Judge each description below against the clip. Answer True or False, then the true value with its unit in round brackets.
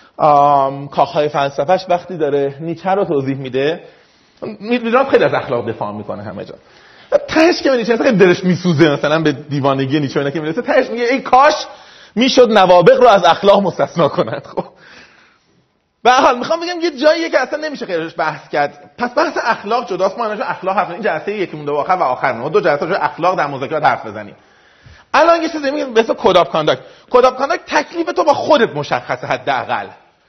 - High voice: True (200 Hz)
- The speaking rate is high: True (185 wpm)